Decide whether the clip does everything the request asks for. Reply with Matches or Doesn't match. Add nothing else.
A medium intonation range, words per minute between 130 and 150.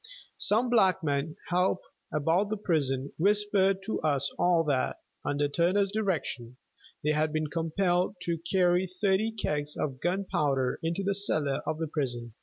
Matches